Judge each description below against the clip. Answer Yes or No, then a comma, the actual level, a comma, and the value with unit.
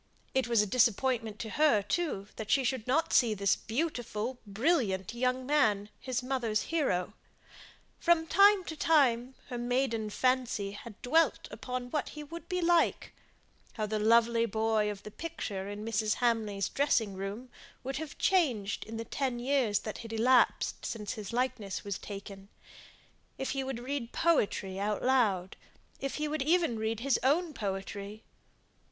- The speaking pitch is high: Yes, high, 235 Hz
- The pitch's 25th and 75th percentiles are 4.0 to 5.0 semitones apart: Yes, average, 4.5 semitones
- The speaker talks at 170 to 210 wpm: No, average, 160 wpm